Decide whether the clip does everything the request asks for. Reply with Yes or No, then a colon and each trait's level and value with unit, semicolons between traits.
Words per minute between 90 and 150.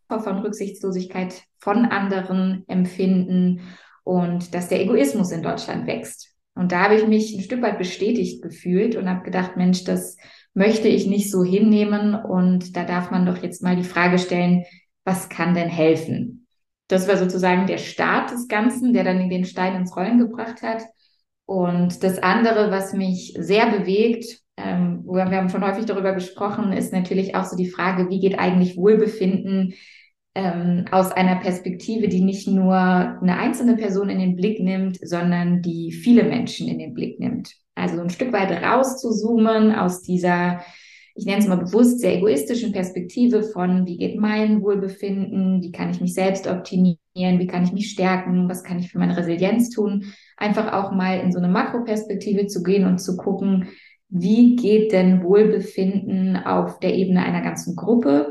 No: average, 170 wpm